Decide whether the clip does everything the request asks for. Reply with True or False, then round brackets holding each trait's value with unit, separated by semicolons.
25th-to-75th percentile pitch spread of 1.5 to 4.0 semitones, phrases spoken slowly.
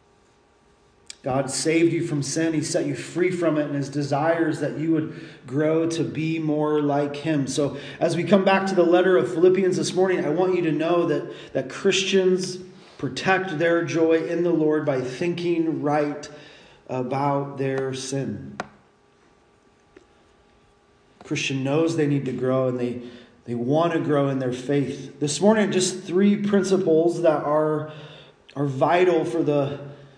False (3.3 semitones; 160 wpm)